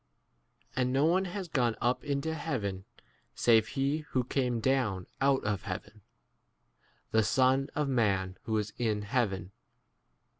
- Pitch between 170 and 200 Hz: No, low, 125 Hz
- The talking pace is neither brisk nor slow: Yes, average, 145 wpm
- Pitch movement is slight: No, average, 4.6 semitones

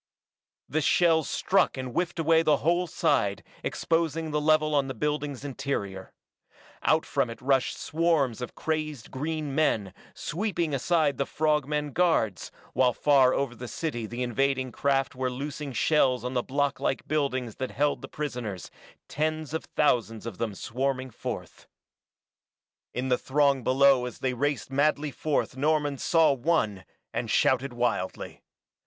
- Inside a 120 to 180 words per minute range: Yes, average, 150 wpm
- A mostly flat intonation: No, average, 3.4 semitones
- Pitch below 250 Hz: Yes, medium, 140 Hz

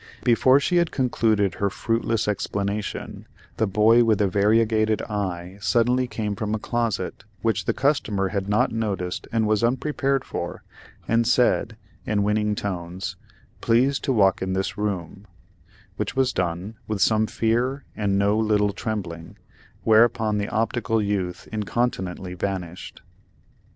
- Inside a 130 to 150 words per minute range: Yes, average, 140 wpm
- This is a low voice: Yes, low, 105 Hz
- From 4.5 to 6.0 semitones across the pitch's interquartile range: No, average, 2.7 semitones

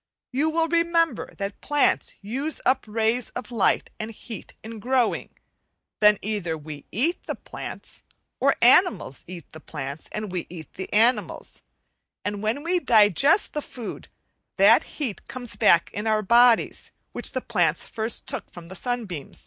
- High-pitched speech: Yes, high, 220 Hz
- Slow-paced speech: No, average, 155 wpm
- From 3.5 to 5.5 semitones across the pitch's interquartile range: Yes, average, 4.8 semitones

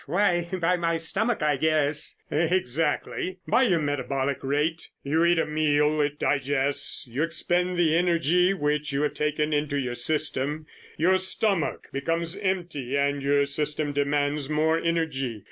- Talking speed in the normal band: Yes, average, 145 wpm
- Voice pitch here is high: No, medium, 150 Hz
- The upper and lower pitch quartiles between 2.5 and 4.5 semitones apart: Yes, average, 2.9 semitones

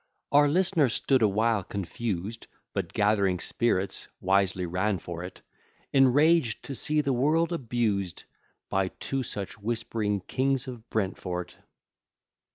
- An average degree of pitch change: No, wide, 5.7 semitones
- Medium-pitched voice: No, low, 110 Hz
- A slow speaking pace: Yes, slow, 115 wpm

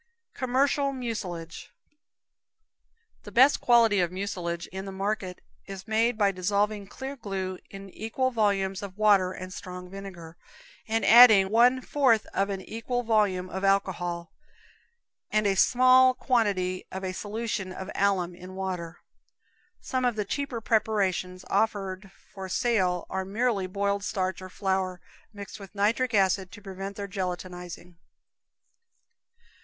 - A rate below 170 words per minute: Yes, slow, 135 wpm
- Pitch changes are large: No, average, 3.1 semitones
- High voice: Yes, high, 195 Hz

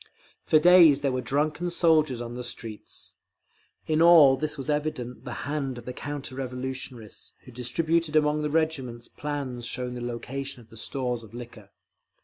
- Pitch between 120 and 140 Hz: Yes, low, 135 Hz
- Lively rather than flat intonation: No, average, 3.7 semitones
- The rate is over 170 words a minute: No, average, 165 wpm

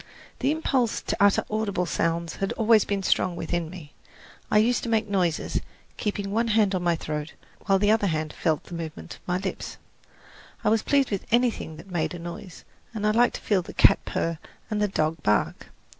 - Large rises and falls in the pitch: No, average, 4.4 semitones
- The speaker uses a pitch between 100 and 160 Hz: No, high, 195 Hz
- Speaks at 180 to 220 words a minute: Yes, average, 200 wpm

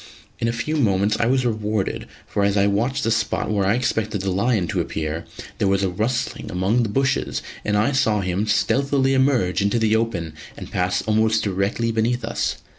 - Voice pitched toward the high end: No, low, 110 Hz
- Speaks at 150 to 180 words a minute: No, average, 195 wpm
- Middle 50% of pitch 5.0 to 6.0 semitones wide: No, average, 3.3 semitones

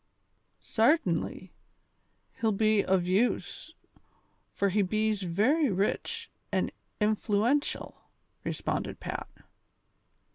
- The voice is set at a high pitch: Yes, high, 215 Hz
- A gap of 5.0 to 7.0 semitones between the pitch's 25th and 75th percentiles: No, average, 3.2 semitones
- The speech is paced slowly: Yes, slow, 80 wpm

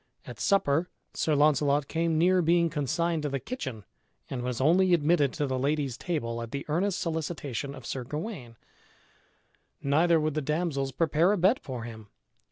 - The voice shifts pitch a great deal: No, average, 3.9 semitones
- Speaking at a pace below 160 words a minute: No, average, 170 wpm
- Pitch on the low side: No, medium, 150 Hz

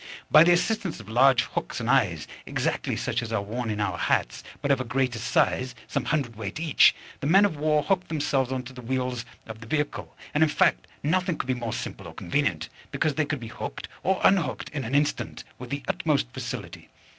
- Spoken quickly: Yes, fast, 215 wpm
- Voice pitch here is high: No, low, 130 Hz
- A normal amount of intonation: Yes, average, 4.4 semitones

